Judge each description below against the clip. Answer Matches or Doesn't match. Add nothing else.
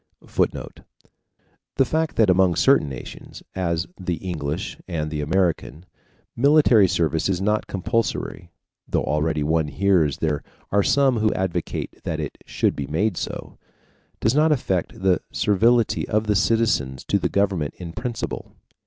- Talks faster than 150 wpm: Doesn't match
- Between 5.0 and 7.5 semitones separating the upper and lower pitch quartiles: Matches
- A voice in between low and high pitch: Doesn't match